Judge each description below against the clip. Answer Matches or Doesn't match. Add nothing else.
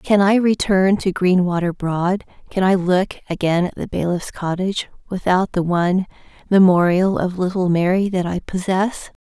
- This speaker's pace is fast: Doesn't match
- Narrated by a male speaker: Doesn't match